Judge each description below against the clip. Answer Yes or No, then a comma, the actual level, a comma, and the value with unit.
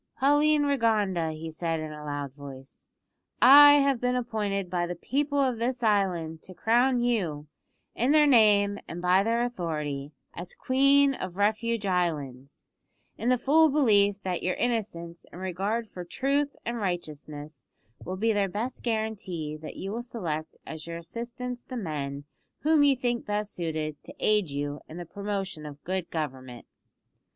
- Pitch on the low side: No, high, 200 Hz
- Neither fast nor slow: Yes, average, 160 wpm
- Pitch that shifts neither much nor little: No, wide, 6.8 semitones